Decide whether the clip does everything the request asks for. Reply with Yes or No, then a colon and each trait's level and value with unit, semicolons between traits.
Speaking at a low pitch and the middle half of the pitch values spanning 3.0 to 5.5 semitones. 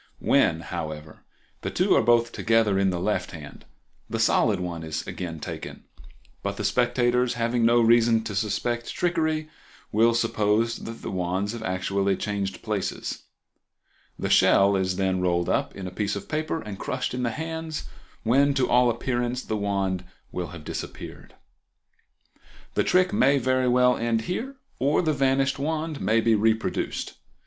Yes: low, 115 Hz; average, 4.4 semitones